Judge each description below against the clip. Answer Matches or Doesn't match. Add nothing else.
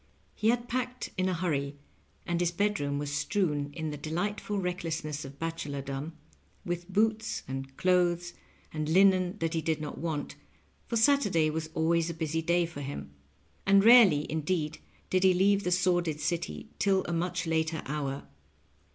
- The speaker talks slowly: Doesn't match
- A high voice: Doesn't match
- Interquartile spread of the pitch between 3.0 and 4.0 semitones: Matches